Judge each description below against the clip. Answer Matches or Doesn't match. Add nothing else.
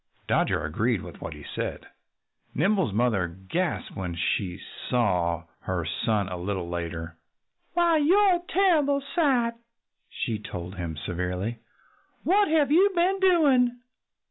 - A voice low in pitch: Matches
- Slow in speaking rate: Matches